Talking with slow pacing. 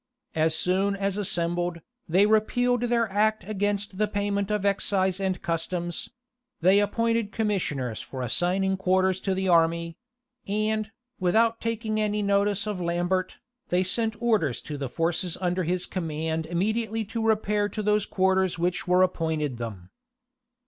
No: average, 145 wpm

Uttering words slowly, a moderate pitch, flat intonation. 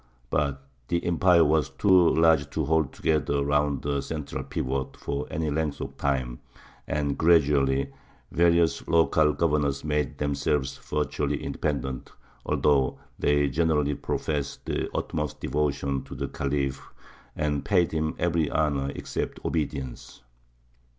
No: slow, 125 wpm; very low, 75 Hz; narrow, 2.3 semitones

